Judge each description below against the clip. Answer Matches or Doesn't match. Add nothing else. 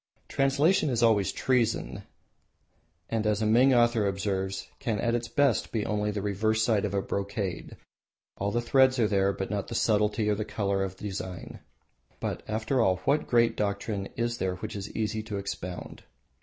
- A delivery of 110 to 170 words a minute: Doesn't match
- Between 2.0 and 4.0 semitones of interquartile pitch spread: Matches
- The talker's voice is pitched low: Matches